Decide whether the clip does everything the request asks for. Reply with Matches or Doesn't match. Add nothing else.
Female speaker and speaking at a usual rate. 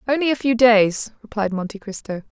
Matches